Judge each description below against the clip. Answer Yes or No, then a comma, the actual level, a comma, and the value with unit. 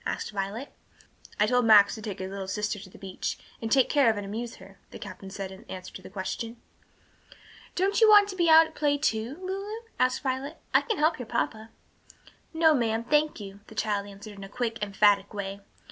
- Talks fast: Yes, fast, 215 wpm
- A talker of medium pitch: No, high, 225 Hz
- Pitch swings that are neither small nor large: No, wide, 6.4 semitones